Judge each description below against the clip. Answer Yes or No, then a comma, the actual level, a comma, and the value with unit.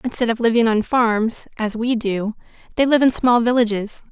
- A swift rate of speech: No, average, 190 wpm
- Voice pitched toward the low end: No, high, 230 Hz